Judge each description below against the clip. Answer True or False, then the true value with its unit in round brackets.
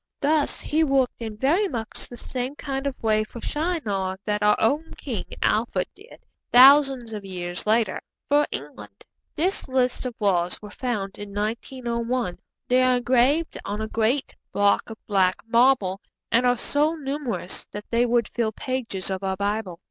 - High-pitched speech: True (235 Hz)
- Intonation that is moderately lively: True (4.6 semitones)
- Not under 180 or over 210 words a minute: False (165 wpm)